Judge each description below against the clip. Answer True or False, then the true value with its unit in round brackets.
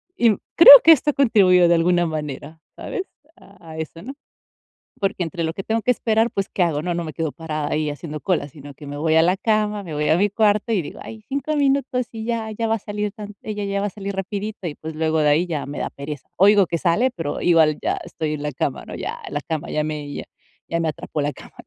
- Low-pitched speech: False (175 Hz)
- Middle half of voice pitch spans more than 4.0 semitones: True (5.3 semitones)